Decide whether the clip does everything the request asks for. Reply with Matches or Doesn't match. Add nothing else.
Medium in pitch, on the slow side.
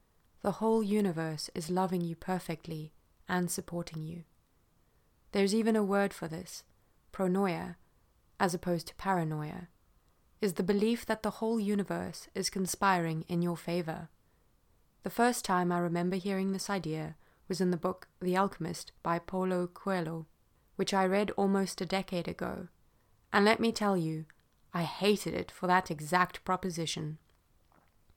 Doesn't match